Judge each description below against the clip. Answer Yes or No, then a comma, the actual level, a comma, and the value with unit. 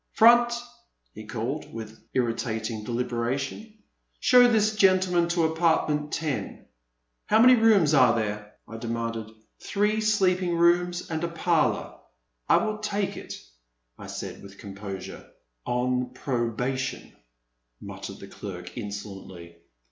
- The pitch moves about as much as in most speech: No, wide, 8.7 semitones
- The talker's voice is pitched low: Yes, low, 130 Hz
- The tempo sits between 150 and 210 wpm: No, slow, 135 wpm